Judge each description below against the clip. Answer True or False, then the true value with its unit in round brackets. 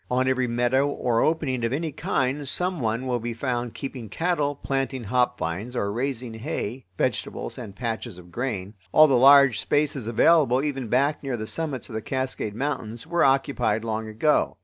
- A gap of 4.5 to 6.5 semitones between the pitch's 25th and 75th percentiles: False (3.6 semitones)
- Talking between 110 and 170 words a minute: False (180 wpm)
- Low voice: True (130 Hz)